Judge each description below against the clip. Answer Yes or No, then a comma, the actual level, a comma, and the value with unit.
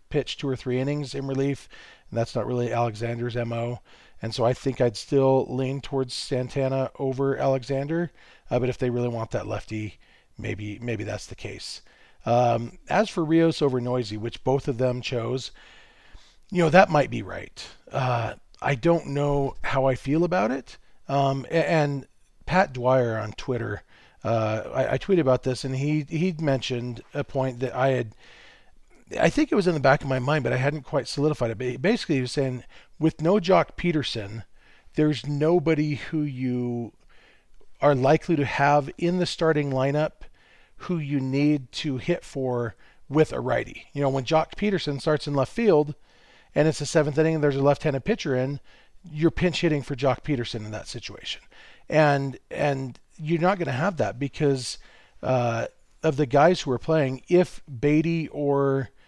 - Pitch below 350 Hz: Yes, low, 135 Hz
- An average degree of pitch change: Yes, average, 3.6 semitones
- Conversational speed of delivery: Yes, average, 180 wpm